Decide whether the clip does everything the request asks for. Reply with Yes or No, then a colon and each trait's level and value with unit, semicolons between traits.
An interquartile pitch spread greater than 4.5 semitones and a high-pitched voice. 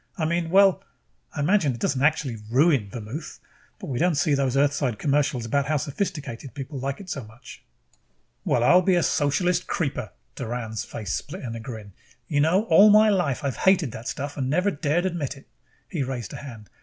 No: wide, 5.4 semitones; medium, 140 Hz